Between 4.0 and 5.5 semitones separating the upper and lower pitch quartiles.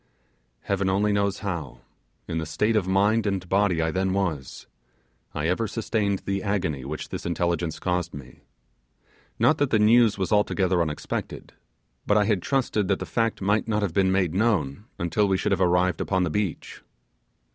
No: average, 3.2 semitones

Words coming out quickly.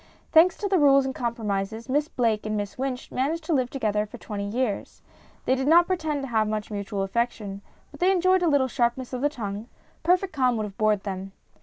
Yes: fast, 215 wpm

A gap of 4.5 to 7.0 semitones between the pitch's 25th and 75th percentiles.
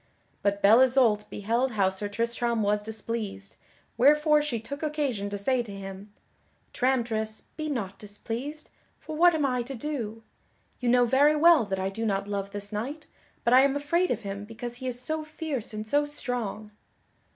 Yes: average, 5.3 semitones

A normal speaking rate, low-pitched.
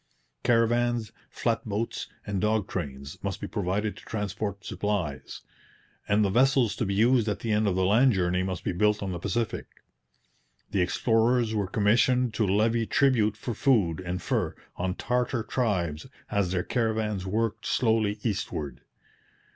Yes: average, 155 wpm; low, 105 Hz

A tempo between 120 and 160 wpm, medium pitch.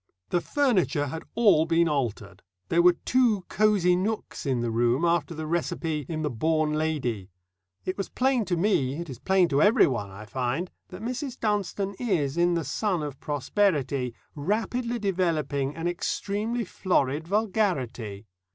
Yes: average, 155 wpm; medium, 165 Hz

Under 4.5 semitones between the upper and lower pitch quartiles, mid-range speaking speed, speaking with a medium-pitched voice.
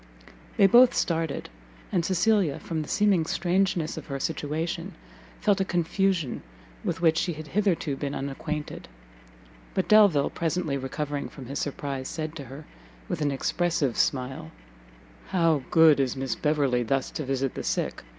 Yes: average, 4.1 semitones; average, 150 wpm; medium, 155 Hz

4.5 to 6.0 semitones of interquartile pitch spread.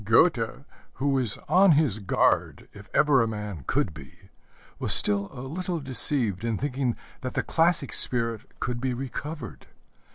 Yes: average, 5.0 semitones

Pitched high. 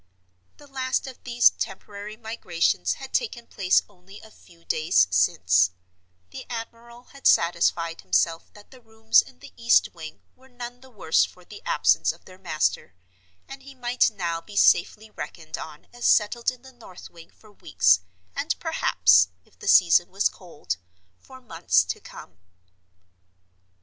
Yes: high, 200 Hz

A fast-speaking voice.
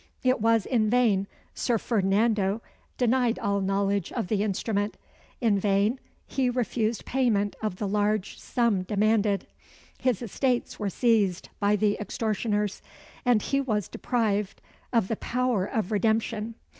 No: slow, 135 wpm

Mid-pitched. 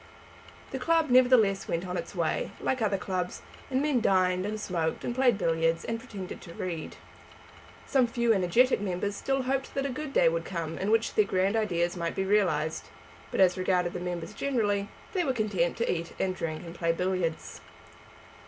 No: high, 195 Hz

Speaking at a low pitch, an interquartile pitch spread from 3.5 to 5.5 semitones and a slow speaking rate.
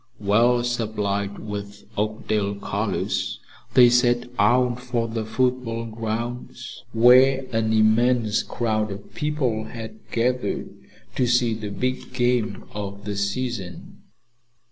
No: low, 115 Hz; narrow, 2.5 semitones; slow, 115 wpm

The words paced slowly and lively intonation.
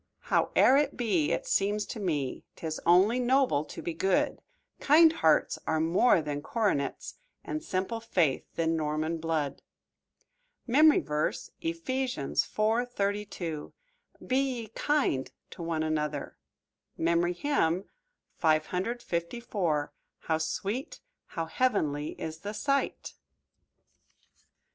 Yes: slow, 110 wpm; wide, 7.0 semitones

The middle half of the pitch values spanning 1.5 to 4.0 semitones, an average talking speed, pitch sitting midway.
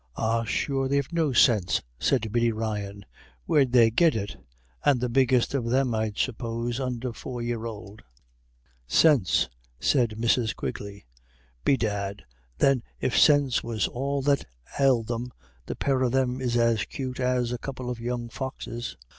No: average, 2.7 semitones; average, 155 wpm; low, 120 Hz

